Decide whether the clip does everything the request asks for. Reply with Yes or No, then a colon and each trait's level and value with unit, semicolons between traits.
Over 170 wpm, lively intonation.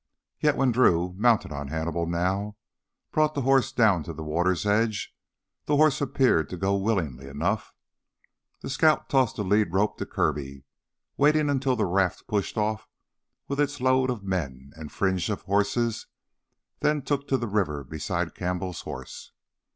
No: average, 160 wpm; wide, 7.1 semitones